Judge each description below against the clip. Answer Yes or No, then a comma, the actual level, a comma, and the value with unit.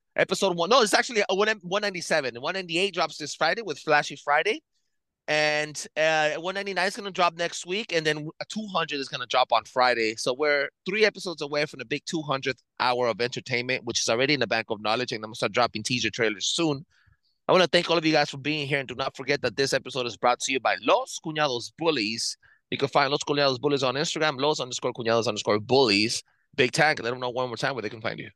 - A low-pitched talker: No, medium, 145 Hz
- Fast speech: Yes, fast, 235 wpm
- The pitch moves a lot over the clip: No, average, 4.8 semitones